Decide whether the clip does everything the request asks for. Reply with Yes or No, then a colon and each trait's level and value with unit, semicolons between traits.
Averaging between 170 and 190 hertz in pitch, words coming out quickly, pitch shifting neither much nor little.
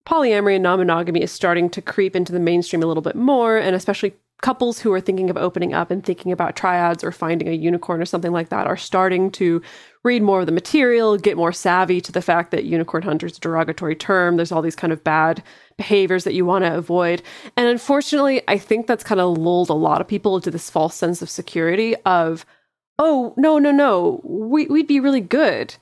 Yes: medium, 185 Hz; fast, 220 wpm; average, 4.5 semitones